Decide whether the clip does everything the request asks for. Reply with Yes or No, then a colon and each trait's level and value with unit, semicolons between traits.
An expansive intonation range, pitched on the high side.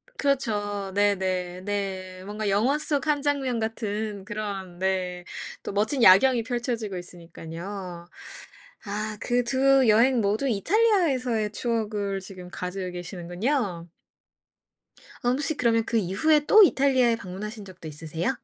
No: average, 5.0 semitones; high, 210 Hz